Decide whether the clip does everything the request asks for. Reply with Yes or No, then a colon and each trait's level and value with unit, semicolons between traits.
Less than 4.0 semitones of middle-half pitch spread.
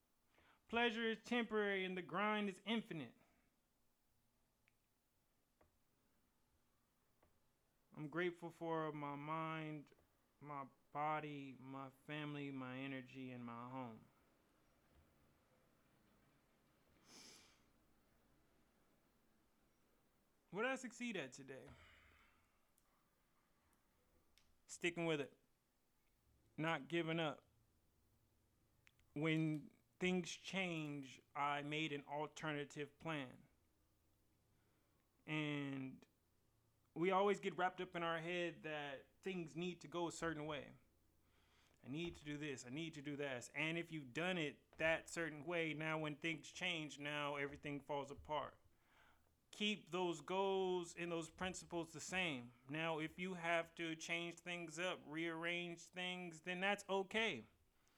No: average, 4.5 semitones